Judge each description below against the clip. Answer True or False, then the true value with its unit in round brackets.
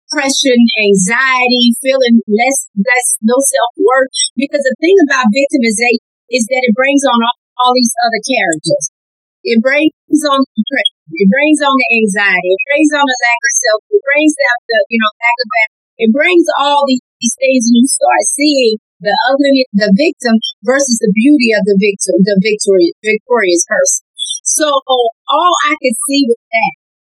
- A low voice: False (250 Hz)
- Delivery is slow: False (175 wpm)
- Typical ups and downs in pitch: True (4.2 semitones)